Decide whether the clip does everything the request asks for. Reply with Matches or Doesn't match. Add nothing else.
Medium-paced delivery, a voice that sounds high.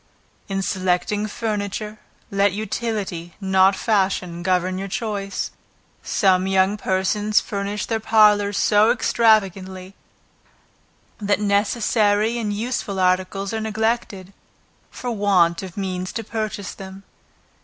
Doesn't match